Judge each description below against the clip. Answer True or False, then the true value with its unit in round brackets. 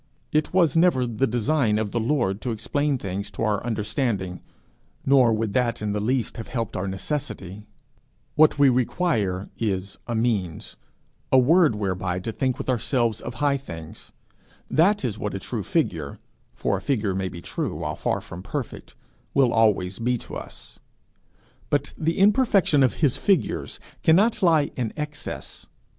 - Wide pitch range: True (6.1 semitones)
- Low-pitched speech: True (120 Hz)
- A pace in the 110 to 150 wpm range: False (165 wpm)